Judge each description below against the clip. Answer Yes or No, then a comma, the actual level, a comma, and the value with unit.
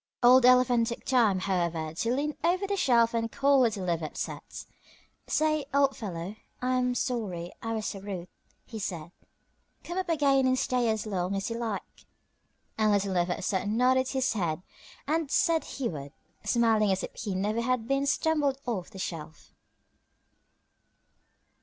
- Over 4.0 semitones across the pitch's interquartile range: Yes, wide, 5.4 semitones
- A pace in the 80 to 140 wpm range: No, average, 165 wpm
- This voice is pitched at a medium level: No, high, 230 Hz